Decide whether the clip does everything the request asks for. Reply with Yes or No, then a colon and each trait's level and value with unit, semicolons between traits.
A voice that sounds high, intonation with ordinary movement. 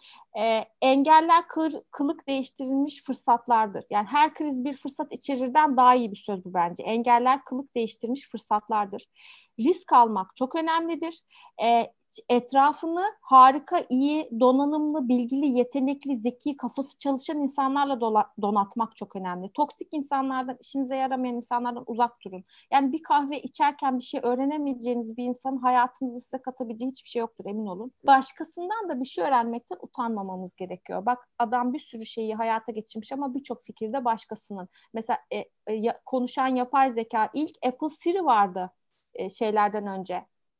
Yes: very high, 255 Hz; average, 3.8 semitones